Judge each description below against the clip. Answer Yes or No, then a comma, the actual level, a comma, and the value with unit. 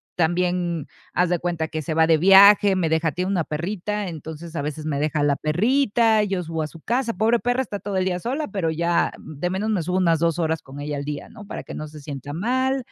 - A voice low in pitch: No, medium, 175 Hz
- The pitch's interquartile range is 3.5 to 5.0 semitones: Yes, average, 4.4 semitones